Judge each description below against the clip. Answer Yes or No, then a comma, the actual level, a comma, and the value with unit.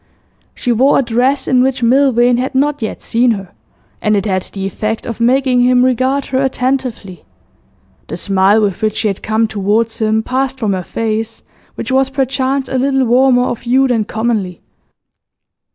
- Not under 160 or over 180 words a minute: Yes, average, 175 wpm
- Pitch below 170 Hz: No, high, 240 Hz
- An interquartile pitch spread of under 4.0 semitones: Yes, average, 3.3 semitones